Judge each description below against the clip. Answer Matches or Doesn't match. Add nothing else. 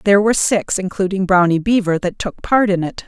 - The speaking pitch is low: Doesn't match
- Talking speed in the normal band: Doesn't match